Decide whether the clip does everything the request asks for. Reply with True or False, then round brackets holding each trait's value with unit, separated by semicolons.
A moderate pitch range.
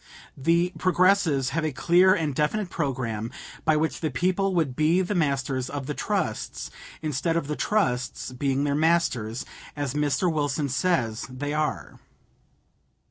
True (4.2 semitones)